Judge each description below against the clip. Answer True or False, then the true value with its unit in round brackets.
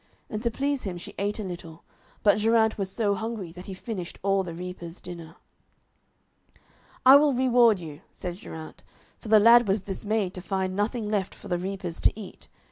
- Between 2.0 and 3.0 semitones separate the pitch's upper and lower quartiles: False (3.6 semitones)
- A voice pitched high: True (195 Hz)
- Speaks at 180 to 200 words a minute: True (190 wpm)